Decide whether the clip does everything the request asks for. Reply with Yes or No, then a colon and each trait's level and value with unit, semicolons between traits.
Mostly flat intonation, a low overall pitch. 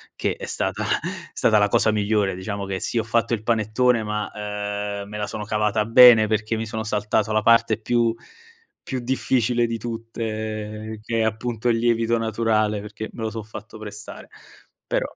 Yes: narrow, 1.4 semitones; low, 110 Hz